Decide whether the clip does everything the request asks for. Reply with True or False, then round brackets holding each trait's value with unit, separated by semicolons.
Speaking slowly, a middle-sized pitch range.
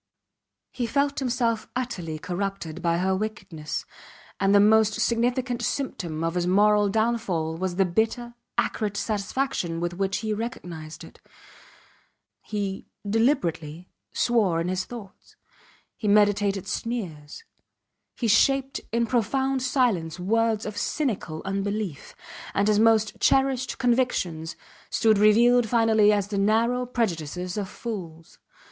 True (125 wpm; 4.5 semitones)